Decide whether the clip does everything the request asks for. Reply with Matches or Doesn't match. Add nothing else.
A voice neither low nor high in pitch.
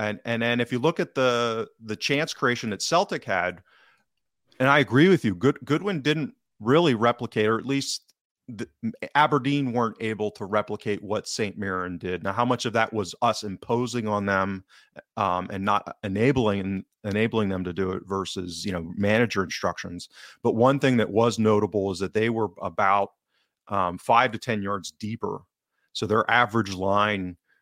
Doesn't match